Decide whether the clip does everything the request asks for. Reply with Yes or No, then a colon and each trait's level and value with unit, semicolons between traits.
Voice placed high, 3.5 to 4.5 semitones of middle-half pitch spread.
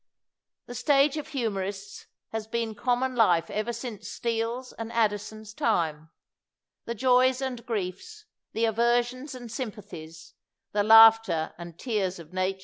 Yes: high, 225 Hz; average, 3.8 semitones